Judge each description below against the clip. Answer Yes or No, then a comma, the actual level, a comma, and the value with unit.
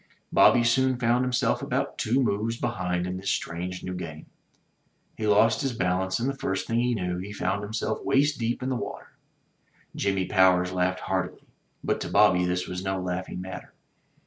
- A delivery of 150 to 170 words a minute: No, average, 180 wpm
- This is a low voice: Yes, very low, 95 Hz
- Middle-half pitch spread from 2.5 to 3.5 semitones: No, average, 4.5 semitones